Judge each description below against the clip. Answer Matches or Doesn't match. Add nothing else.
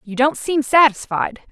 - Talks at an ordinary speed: Matches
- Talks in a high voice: Matches